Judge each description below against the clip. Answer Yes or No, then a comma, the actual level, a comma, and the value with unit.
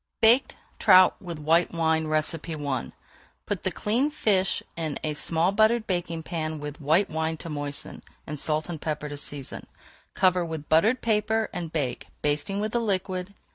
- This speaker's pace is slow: No, average, 165 wpm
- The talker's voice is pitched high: No, medium, 165 Hz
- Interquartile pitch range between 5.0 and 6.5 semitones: No, average, 4.3 semitones